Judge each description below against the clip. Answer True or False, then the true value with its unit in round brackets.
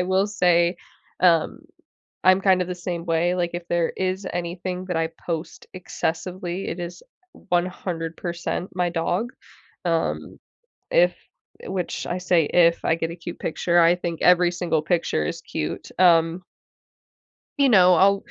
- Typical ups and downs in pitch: False (1.5 semitones)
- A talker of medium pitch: True (175 Hz)